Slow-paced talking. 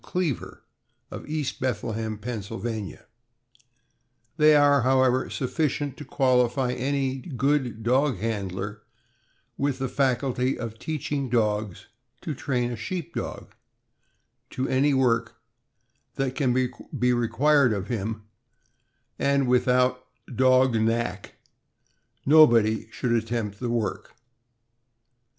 Yes: slow, 105 wpm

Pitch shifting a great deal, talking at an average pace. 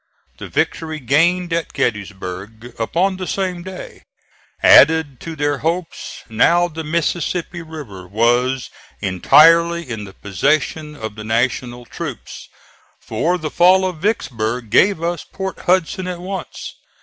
No: wide, 6.8 semitones; slow, 130 wpm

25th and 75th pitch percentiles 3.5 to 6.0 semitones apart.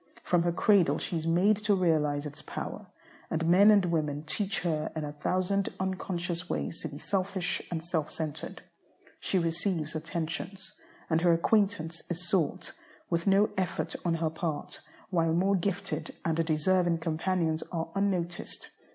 No: average, 2.8 semitones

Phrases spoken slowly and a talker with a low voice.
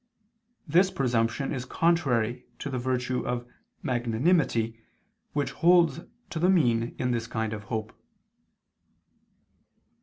Yes: slow, 115 wpm; low, 125 Hz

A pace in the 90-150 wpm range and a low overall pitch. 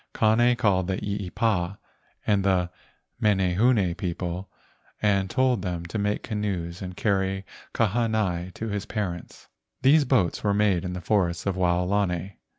Yes: average, 145 wpm; very low, 95 Hz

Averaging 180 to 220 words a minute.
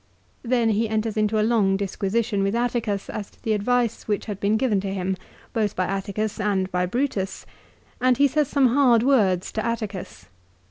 Yes: average, 190 wpm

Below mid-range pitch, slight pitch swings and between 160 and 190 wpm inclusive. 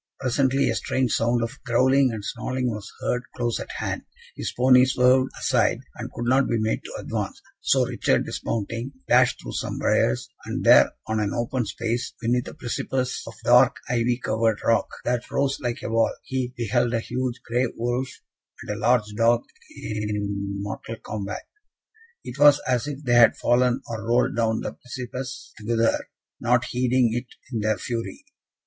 Yes: low, 120 Hz; narrow, 1.9 semitones; average, 170 wpm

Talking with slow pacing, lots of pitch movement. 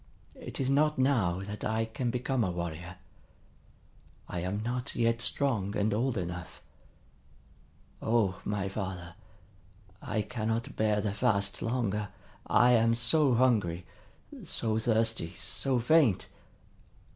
No: slow, 120 wpm; average, 3.9 semitones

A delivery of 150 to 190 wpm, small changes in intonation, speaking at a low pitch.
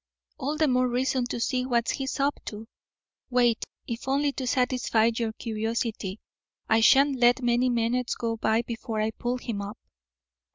No: average, 165 wpm; narrow, 2.1 semitones; high, 240 Hz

